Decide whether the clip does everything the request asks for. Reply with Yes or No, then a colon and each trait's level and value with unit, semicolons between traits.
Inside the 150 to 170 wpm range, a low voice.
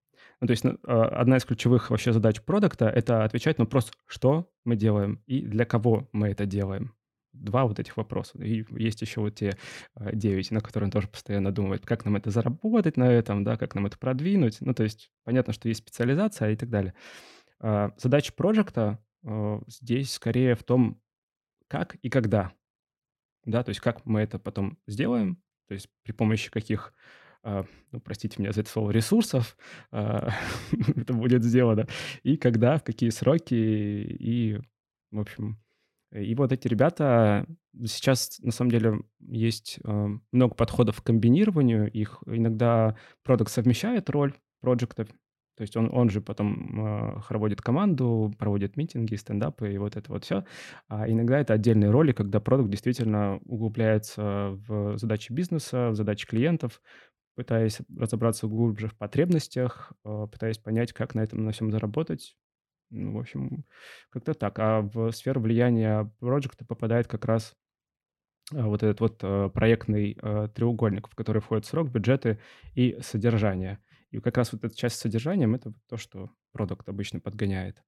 Yes: fast, 160 wpm; low, 115 Hz